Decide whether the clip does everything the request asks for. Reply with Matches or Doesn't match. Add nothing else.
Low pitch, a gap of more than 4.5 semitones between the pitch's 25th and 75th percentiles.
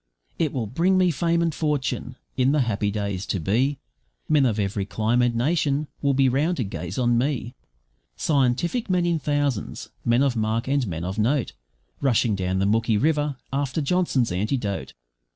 Matches